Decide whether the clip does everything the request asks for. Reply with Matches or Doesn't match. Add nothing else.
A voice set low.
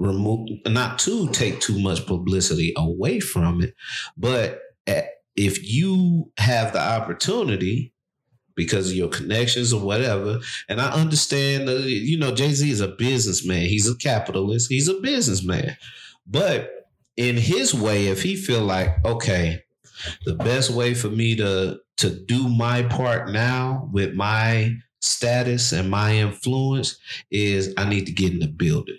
Matches